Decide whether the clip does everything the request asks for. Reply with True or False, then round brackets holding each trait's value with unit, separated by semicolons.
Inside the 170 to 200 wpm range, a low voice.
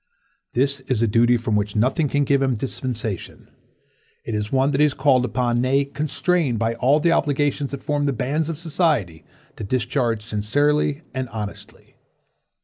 True (175 wpm; 130 Hz)